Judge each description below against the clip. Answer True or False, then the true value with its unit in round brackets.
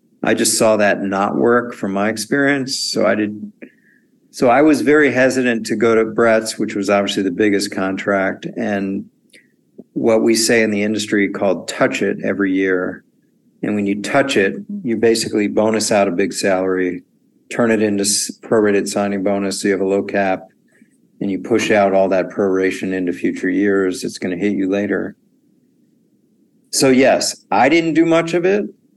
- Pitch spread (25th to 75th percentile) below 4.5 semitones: False (4.8 semitones)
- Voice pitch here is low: True (110 Hz)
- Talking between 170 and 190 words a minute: True (180 wpm)